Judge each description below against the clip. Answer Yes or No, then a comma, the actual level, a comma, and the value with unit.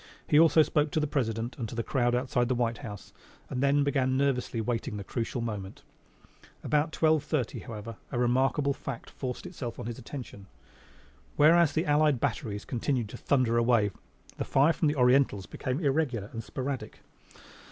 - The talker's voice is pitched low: Yes, low, 130 Hz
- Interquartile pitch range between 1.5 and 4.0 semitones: Yes, average, 3.7 semitones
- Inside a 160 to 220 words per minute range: Yes, average, 175 wpm